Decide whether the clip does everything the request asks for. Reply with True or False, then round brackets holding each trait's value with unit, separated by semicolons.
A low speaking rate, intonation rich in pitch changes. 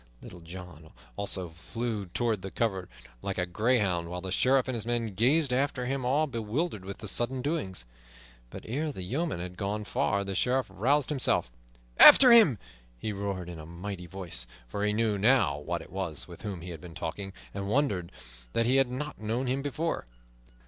False (190 wpm; 6.0 semitones)